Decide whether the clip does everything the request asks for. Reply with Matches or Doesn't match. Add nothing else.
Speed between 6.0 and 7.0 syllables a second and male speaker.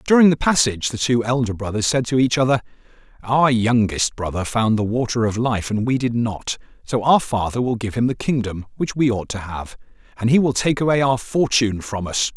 Doesn't match